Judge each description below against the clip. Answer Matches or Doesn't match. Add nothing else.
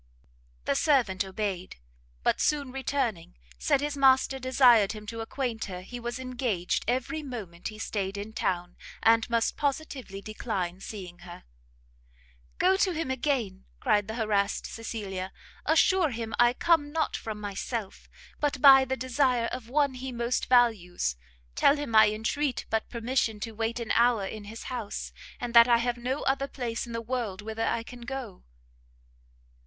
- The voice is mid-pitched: Doesn't match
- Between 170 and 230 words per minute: Doesn't match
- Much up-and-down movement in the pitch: Doesn't match